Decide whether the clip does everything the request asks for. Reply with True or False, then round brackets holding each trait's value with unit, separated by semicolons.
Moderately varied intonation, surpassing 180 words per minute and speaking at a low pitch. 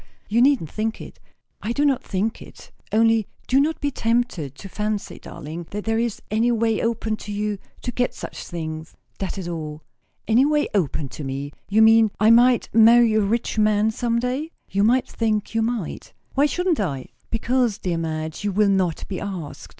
False (3.9 semitones; 190 wpm; 215 Hz)